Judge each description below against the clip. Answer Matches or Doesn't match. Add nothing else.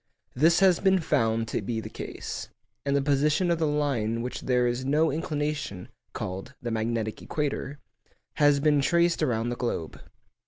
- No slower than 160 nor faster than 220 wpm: Matches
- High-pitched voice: Doesn't match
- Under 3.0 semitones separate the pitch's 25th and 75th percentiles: Doesn't match